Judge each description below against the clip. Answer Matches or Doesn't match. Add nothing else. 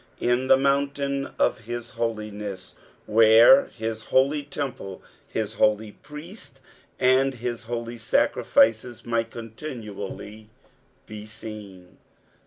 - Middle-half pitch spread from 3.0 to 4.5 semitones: Matches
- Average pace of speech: Doesn't match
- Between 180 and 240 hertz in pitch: Doesn't match